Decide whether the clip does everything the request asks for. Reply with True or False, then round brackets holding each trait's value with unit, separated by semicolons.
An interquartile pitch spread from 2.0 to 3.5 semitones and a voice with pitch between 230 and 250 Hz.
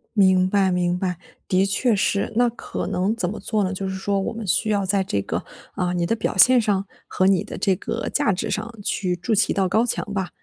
False (2.6 semitones; 195 Hz)